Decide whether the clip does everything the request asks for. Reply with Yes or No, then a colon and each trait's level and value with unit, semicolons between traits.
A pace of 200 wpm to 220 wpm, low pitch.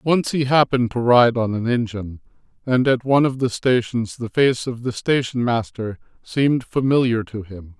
No: average, 185 wpm; low, 120 Hz